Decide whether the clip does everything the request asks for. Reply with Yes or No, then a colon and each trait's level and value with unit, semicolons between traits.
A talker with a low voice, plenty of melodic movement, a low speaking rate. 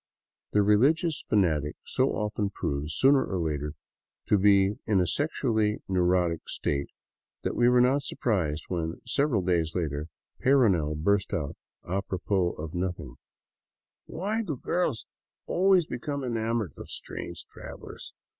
Yes: low, 100 Hz; wide, 7.0 semitones; slow, 130 wpm